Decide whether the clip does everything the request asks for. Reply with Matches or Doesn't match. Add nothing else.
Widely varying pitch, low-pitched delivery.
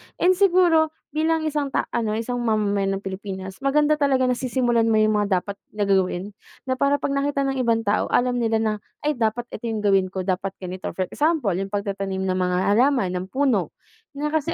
Doesn't match